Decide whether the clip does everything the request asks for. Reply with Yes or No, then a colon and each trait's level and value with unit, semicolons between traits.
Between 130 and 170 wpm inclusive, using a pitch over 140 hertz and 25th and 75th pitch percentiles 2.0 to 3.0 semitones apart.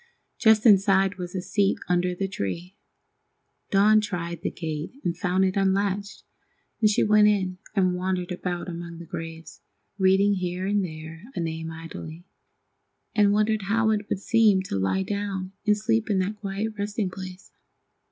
Yes: average, 160 wpm; high, 190 Hz; narrow, 2.6 semitones